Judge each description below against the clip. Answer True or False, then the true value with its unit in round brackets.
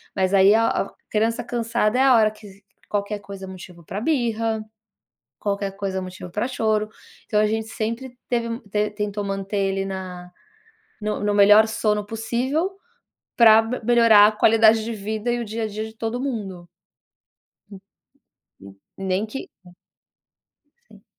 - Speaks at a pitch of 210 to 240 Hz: True (215 Hz)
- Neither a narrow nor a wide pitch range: False (2.3 semitones)